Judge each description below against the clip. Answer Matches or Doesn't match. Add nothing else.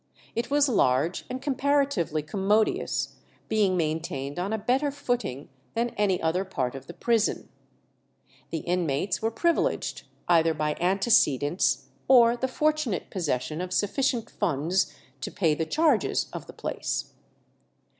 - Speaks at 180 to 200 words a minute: Doesn't match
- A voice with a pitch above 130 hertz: Matches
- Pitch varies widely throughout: Matches